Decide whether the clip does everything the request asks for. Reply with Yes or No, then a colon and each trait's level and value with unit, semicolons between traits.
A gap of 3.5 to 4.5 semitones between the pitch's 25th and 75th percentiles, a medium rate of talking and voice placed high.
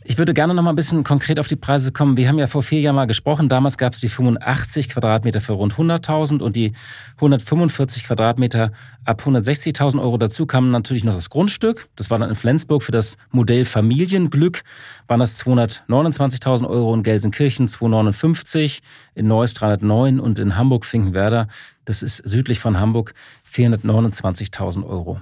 No: average, 4.2 semitones; average, 170 wpm; low, 125 Hz